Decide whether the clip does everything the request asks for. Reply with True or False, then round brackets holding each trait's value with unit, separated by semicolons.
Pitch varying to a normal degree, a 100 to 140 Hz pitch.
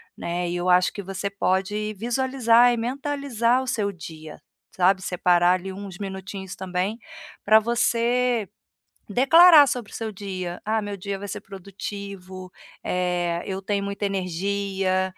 False (3.5 semitones; 200 Hz)